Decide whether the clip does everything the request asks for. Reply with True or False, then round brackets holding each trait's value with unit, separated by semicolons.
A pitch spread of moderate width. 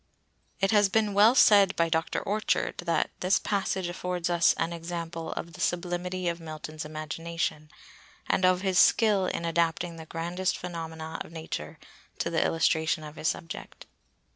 False (2.1 semitones)